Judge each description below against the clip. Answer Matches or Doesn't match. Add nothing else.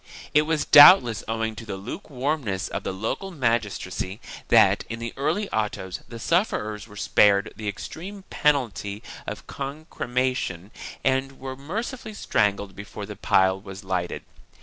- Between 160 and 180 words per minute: Doesn't match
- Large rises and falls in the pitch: Matches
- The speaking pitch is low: Matches